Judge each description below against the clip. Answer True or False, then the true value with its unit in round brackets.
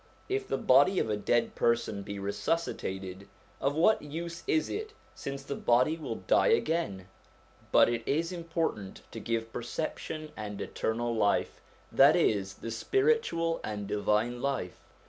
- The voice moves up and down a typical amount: False (8.0 semitones)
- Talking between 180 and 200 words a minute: False (145 wpm)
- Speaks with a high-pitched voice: False (120 Hz)